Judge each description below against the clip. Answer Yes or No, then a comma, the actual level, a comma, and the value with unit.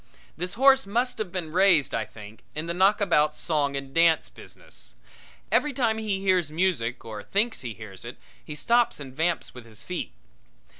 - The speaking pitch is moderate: Yes, medium, 170 Hz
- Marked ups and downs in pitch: Yes, wide, 6.8 semitones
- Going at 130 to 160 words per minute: No, average, 180 wpm